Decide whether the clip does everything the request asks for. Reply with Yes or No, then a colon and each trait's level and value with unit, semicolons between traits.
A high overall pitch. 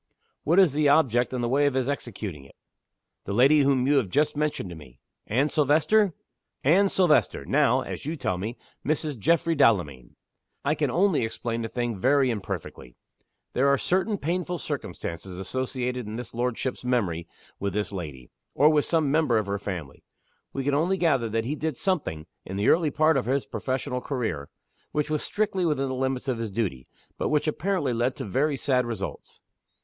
No: low, 130 Hz